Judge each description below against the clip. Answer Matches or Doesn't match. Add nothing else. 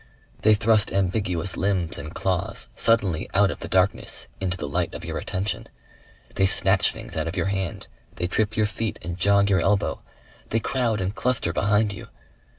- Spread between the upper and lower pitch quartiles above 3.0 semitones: Doesn't match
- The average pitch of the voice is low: Matches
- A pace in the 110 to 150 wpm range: Doesn't match